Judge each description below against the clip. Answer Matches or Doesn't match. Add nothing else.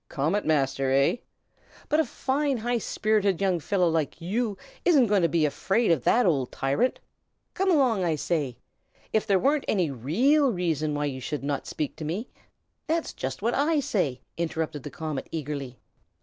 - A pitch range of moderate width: Doesn't match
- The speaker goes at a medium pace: Matches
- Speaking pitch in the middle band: Matches